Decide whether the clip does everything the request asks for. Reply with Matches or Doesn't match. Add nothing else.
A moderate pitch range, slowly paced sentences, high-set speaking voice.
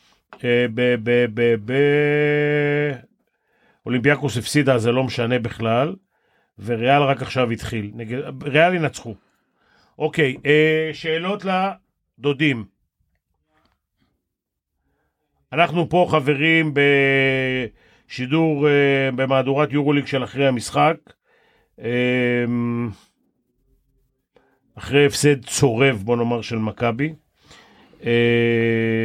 Doesn't match